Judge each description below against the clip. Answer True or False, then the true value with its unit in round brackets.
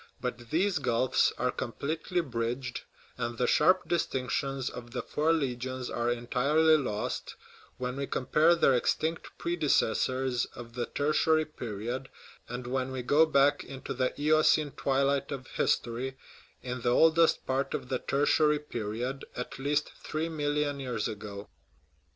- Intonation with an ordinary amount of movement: True (3.5 semitones)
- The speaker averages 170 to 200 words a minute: False (140 wpm)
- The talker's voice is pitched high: False (135 Hz)